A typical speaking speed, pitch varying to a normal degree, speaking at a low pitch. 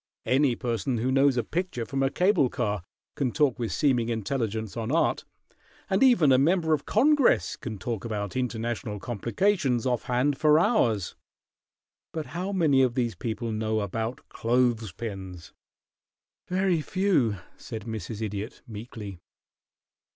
Yes: average, 145 wpm; average, 4.8 semitones; low, 120 Hz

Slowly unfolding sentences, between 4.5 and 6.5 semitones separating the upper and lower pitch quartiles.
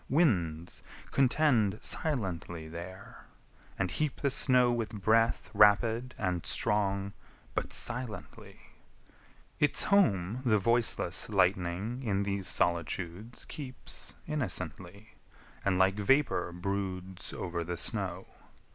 Yes: slow, 100 wpm; average, 4.9 semitones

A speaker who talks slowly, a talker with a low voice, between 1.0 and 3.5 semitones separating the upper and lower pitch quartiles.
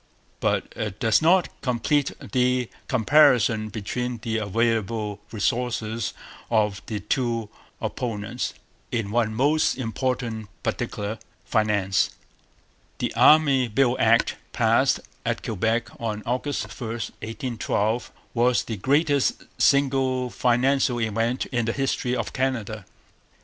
Yes: slow, 110 wpm; low, 120 Hz; average, 2.9 semitones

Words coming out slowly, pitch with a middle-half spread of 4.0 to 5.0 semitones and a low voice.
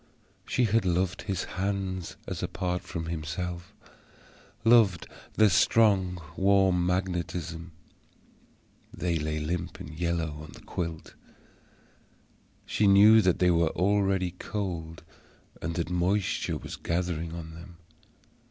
No: slow, 115 wpm; narrow, 2.6 semitones; very low, 90 Hz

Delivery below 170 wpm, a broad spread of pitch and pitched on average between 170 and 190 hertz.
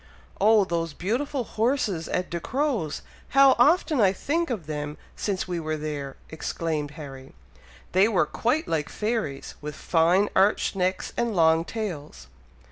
Yes: average, 140 wpm; wide, 6.6 semitones; medium, 185 Hz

